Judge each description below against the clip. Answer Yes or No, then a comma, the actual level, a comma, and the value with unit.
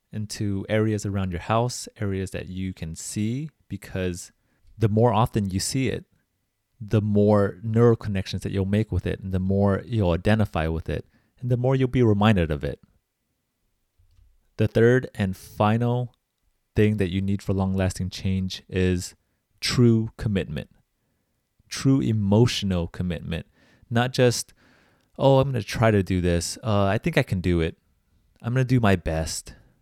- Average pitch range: Yes, average, 3.6 semitones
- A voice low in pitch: Yes, low, 100 Hz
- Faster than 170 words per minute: No, average, 160 wpm